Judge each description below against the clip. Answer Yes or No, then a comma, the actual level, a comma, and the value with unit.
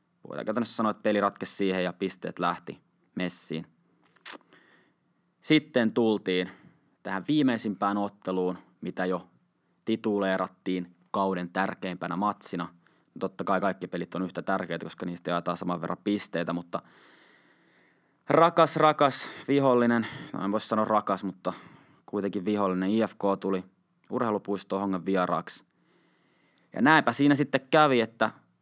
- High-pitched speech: No, very low, 95 Hz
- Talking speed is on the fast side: No, average, 120 wpm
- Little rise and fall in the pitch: No, average, 3.5 semitones